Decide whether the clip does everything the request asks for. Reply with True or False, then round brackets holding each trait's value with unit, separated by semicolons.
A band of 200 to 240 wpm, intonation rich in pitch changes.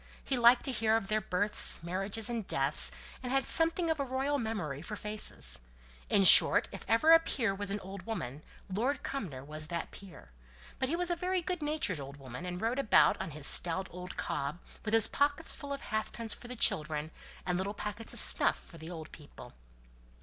True (205 wpm; 7.2 semitones)